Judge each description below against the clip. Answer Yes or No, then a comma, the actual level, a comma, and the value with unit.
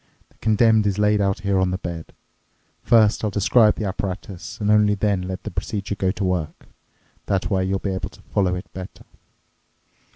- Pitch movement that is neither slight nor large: No, narrow, 2.0 semitones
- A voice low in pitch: Yes, low, 100 Hz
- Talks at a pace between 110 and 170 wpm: No, average, 190 wpm